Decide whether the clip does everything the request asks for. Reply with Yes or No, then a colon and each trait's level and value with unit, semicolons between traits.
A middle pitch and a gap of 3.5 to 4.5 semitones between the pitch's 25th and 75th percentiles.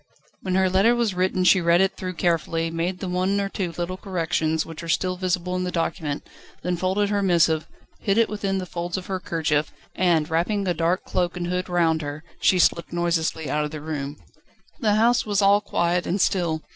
No: medium, 180 Hz; narrow, 2.4 semitones